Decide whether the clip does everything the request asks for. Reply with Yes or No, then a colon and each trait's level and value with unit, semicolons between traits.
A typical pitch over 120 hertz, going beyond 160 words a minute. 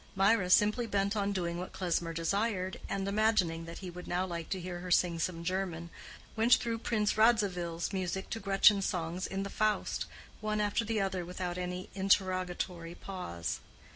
Yes: medium, 185 Hz; average, 170 wpm